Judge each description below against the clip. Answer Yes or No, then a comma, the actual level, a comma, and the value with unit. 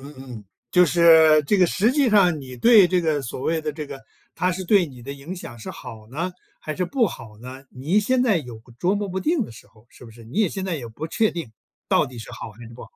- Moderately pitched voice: Yes, medium, 160 Hz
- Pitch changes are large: Yes, wide, 6.9 semitones